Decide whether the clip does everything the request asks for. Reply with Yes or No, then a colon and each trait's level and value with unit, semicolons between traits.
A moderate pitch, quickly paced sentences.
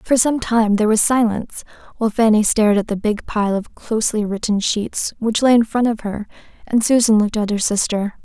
No: high, 220 Hz; fast, 210 wpm